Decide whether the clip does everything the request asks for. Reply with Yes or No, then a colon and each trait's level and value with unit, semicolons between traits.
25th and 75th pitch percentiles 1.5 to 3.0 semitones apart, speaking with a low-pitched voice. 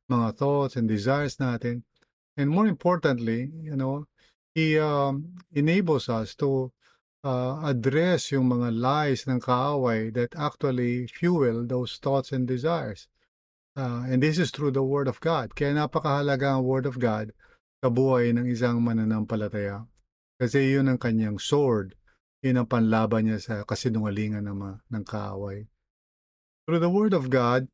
No: average, 3.7 semitones; low, 130 Hz